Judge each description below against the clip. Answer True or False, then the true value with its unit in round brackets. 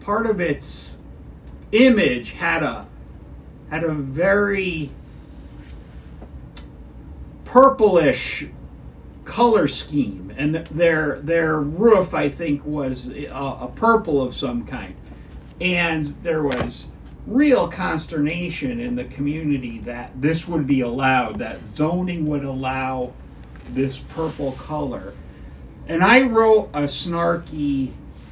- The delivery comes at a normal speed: False (105 wpm)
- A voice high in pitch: False (145 Hz)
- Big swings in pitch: True (8.2 semitones)